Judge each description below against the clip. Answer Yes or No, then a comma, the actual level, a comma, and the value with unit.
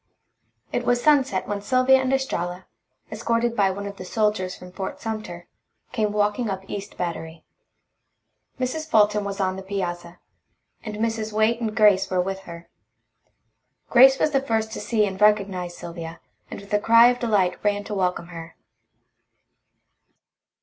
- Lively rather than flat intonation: No, average, 3.6 semitones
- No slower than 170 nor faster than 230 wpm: No, average, 155 wpm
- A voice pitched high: Yes, high, 205 Hz